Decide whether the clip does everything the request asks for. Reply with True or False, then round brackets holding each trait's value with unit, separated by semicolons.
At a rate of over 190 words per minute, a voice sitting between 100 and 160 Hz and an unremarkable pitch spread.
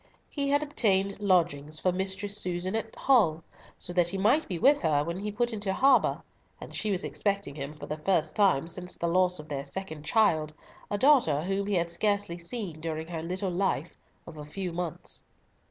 False (200 wpm; 180 Hz; 4.2 semitones)